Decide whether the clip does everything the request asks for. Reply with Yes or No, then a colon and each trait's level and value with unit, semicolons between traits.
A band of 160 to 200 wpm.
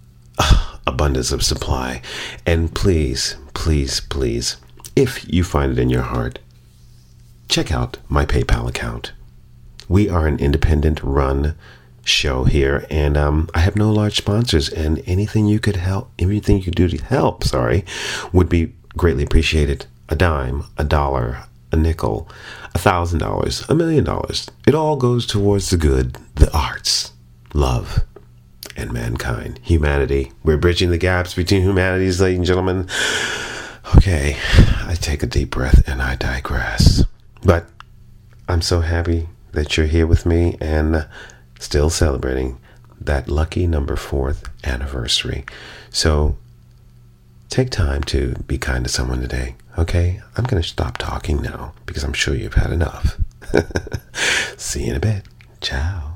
No: average, 145 wpm